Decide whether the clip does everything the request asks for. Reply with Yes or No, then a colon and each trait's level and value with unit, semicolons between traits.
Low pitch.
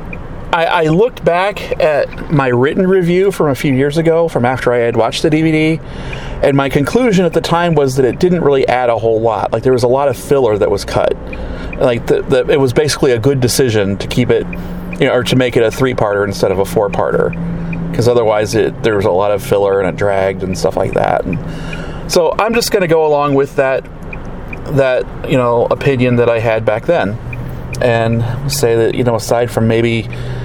Yes: low, 130 Hz